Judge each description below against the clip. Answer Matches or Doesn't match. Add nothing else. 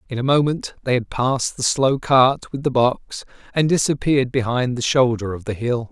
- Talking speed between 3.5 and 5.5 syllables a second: Matches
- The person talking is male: Matches